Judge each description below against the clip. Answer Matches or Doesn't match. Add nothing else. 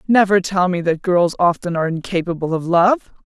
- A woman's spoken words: Matches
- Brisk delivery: Doesn't match